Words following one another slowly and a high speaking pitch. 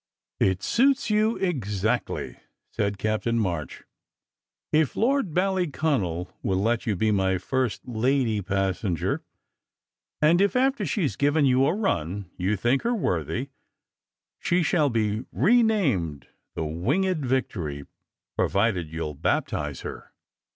No: slow, 125 wpm; low, 115 Hz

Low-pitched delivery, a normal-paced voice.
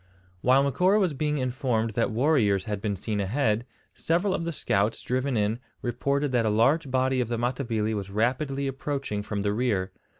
Yes: low, 125 Hz; average, 180 wpm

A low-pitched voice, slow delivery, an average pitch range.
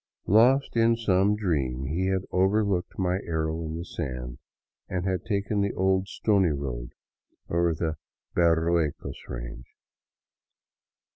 Yes: very low, 90 Hz; slow, 120 wpm; average, 4.0 semitones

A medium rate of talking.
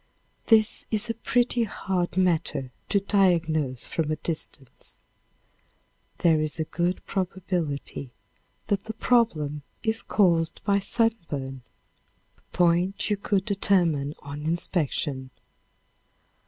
No: slow, 110 wpm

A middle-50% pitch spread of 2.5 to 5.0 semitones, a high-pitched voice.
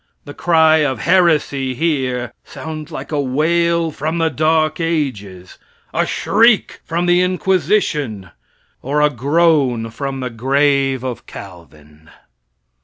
No: average, 4.4 semitones; medium, 145 Hz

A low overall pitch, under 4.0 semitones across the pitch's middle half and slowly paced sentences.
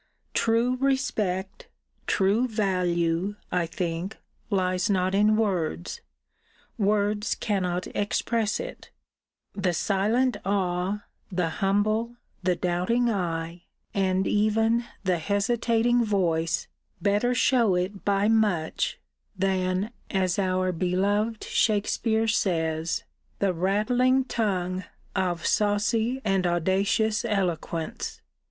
No: high, 195 Hz; average, 3.3 semitones; slow, 95 wpm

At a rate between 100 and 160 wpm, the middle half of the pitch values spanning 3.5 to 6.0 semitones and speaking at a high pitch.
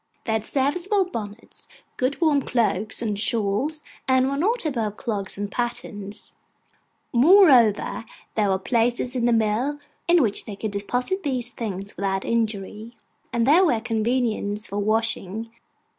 Yes: average, 145 wpm; average, 3.9 semitones; high, 230 Hz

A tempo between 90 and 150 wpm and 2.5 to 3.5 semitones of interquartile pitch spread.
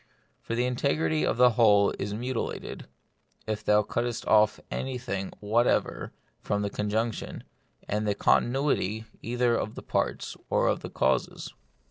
Yes: average, 140 wpm; average, 2.9 semitones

